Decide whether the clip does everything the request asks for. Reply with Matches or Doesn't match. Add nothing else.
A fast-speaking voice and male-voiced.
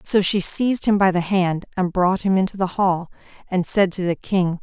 Doesn't match